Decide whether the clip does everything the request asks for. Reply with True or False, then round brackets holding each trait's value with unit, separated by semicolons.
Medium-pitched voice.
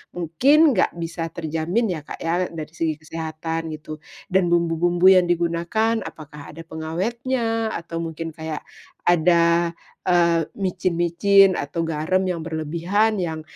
True (170 Hz)